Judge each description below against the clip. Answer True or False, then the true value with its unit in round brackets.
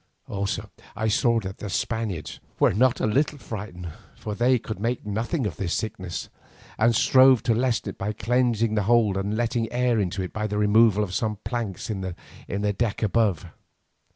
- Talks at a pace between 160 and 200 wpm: True (180 wpm)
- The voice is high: False (110 Hz)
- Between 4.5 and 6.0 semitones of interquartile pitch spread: False (3.0 semitones)